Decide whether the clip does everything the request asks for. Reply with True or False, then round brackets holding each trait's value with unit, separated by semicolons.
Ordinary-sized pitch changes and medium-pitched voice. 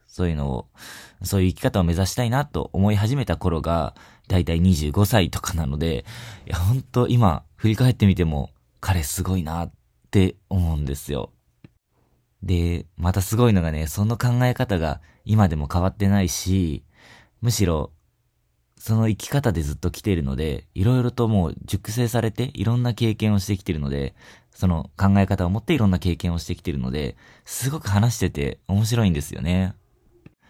False (4.7 semitones; 95 Hz)